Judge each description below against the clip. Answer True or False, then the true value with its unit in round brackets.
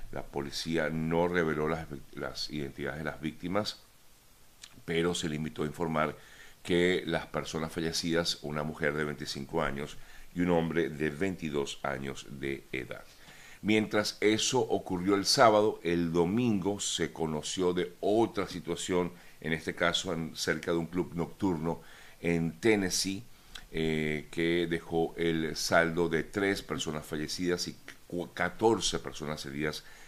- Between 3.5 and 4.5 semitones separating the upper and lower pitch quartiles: False (2.6 semitones)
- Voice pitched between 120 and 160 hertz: False (85 Hz)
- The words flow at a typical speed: True (140 wpm)